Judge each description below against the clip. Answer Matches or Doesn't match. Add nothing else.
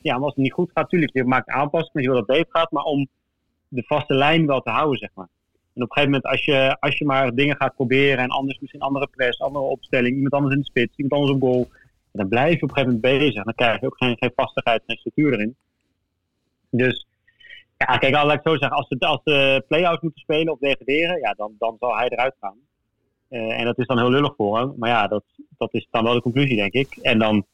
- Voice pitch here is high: Doesn't match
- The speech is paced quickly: Matches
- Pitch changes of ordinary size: Matches